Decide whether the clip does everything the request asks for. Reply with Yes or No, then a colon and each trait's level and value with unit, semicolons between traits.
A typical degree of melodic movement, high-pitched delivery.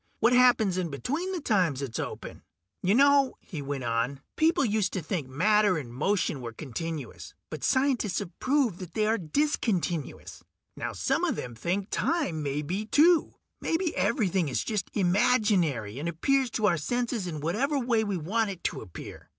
No: wide, 7.9 semitones; high, 195 Hz